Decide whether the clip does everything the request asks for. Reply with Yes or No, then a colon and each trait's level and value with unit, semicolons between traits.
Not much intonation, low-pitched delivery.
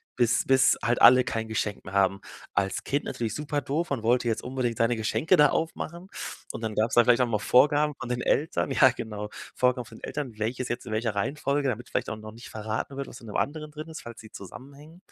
No: average, 4.3 semitones; low, 125 Hz